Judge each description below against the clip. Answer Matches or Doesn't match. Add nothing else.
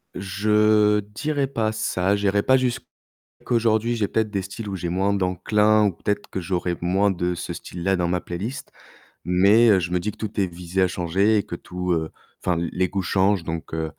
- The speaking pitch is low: Matches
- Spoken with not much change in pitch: Doesn't match